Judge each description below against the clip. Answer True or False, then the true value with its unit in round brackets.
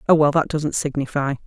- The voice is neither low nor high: True (145 Hz)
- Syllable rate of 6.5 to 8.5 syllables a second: False (5.6 syllables/s)